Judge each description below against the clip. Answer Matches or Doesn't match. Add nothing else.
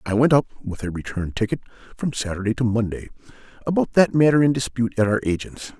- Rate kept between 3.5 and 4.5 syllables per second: Doesn't match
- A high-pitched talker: Doesn't match